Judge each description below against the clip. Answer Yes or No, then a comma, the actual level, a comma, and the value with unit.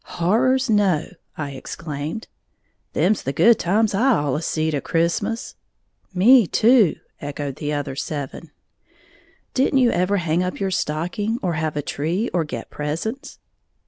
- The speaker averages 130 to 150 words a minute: Yes, average, 145 wpm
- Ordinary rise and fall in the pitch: No, wide, 6.6 semitones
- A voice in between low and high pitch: Yes, medium, 175 Hz